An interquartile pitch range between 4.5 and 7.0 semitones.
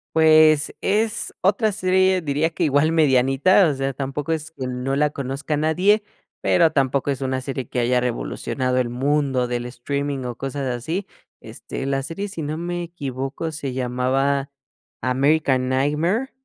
No: average, 3.7 semitones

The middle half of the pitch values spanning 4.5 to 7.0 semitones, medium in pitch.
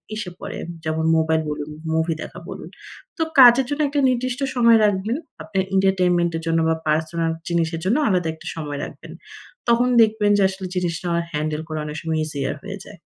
Yes: average, 5.1 semitones; medium, 180 Hz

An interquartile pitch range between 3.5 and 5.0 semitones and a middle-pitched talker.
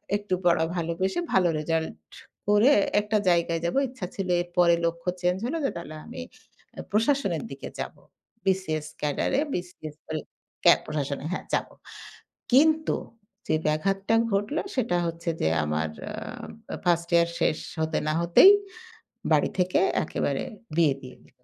Yes: average, 4.0 semitones; medium, 170 Hz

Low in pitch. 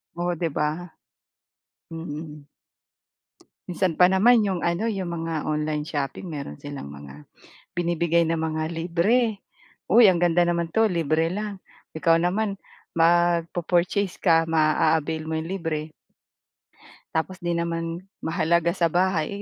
No: medium, 170 Hz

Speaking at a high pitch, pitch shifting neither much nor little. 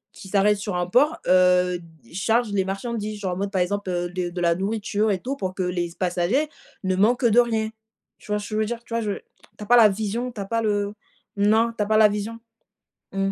Yes: high, 205 Hz; average, 3.3 semitones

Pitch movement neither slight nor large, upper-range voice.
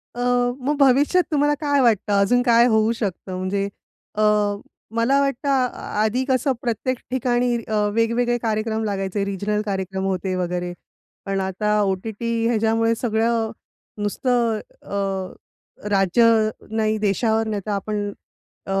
Yes: average, 3.4 semitones; high, 220 Hz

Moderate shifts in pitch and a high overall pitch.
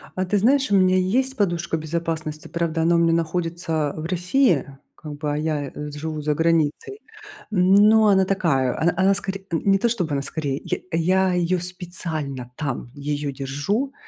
No: average, 3.9 semitones; medium, 170 Hz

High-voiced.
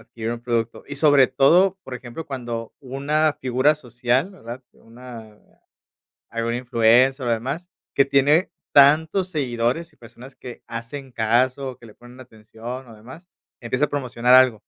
No: low, 125 Hz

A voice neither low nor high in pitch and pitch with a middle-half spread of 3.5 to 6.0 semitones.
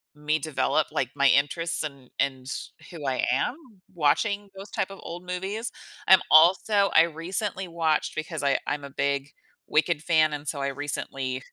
Yes: medium, 155 Hz; average, 4.4 semitones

